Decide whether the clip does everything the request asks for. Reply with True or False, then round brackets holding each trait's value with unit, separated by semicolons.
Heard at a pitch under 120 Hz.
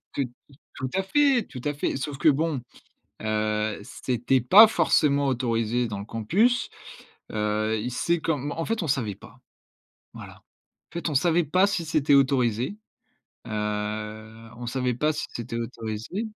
False (130 Hz)